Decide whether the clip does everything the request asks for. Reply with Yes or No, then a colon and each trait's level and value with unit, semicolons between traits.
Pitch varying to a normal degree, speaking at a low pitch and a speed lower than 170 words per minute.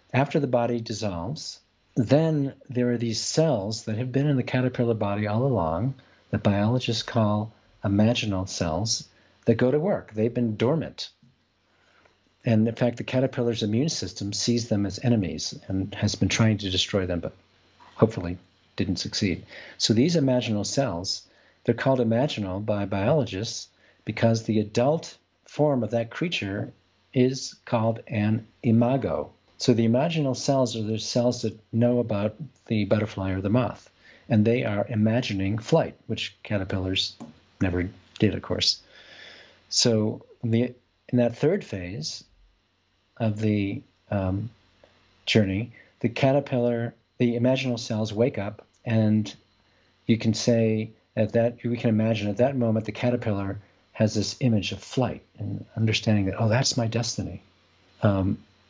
Yes: average, 3.2 semitones; low, 110 Hz; average, 145 wpm